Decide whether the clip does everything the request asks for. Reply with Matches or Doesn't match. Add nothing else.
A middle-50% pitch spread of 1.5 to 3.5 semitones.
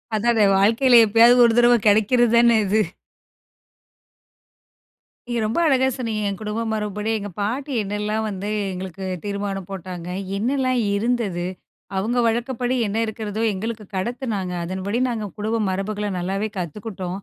Matches